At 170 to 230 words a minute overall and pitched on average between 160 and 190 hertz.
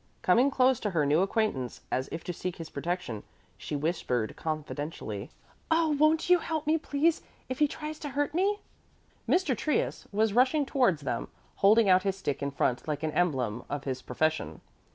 Yes: average, 180 wpm; medium, 185 Hz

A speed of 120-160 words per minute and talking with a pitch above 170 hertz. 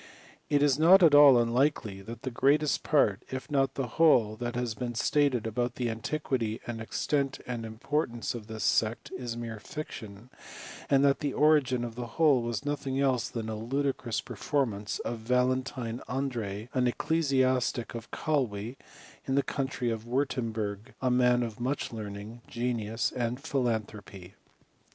No: average, 155 wpm; low, 125 Hz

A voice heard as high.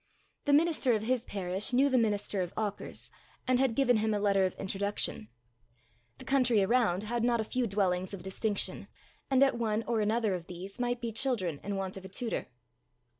Yes: high, 215 Hz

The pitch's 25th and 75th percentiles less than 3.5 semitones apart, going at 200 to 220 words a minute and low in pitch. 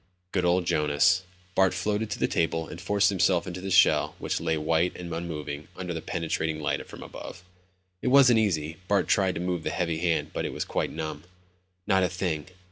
Yes: average, 2.7 semitones; fast, 205 wpm; very low, 90 Hz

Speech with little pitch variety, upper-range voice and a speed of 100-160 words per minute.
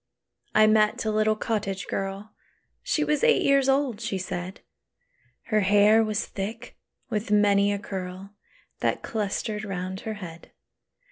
Yes: narrow, 2.1 semitones; high, 210 Hz; average, 140 wpm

